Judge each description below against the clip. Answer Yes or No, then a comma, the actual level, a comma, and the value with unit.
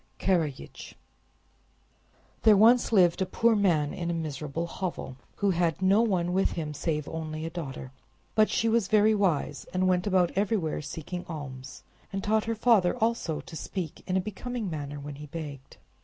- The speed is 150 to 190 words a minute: Yes, average, 170 wpm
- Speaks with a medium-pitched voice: Yes, medium, 175 Hz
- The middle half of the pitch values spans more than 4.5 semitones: Yes, average, 4.9 semitones